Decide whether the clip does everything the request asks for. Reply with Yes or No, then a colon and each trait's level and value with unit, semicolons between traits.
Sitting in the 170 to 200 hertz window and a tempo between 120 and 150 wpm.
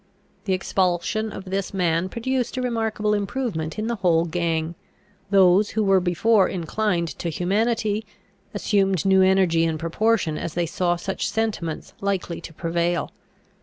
Yes: high, 190 Hz; average, 145 wpm